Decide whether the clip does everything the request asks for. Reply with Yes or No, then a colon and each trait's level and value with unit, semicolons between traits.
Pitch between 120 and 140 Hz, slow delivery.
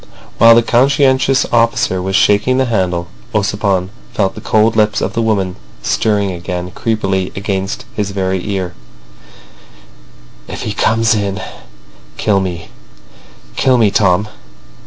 No: low, 100 Hz; slow, 125 wpm